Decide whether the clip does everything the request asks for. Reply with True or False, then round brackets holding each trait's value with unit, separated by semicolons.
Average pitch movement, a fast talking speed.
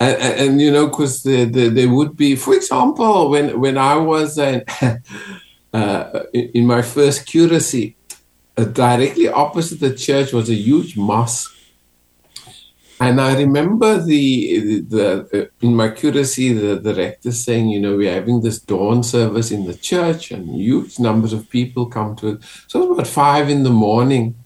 False (4.4 semitones; 180 wpm)